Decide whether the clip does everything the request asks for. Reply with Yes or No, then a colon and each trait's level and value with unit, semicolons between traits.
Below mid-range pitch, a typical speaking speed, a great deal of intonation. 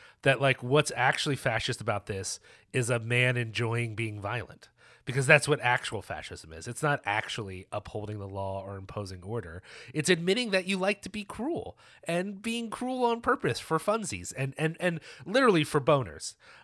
Yes: low, 130 Hz; average, 175 wpm; wide, 7.3 semitones